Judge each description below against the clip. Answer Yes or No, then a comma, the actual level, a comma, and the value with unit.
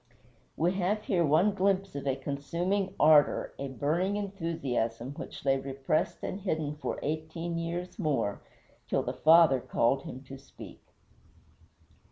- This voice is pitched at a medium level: Yes, medium, 160 Hz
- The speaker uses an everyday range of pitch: Yes, average, 4.9 semitones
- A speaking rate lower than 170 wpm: Yes, average, 140 wpm